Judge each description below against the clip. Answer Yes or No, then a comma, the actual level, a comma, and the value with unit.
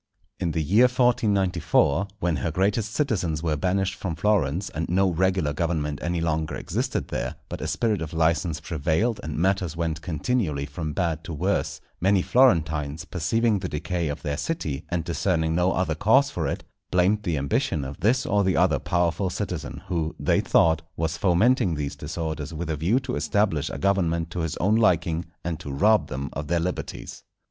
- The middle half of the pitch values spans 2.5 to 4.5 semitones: Yes, average, 3.8 semitones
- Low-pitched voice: Yes, very low, 85 Hz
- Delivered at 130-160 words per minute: No, average, 185 wpm